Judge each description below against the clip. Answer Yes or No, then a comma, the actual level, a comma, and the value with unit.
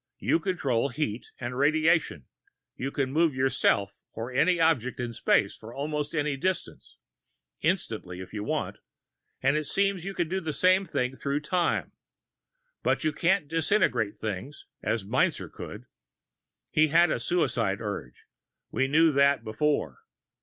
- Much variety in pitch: Yes, wide, 5.7 semitones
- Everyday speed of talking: Yes, average, 145 wpm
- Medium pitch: Yes, medium, 145 Hz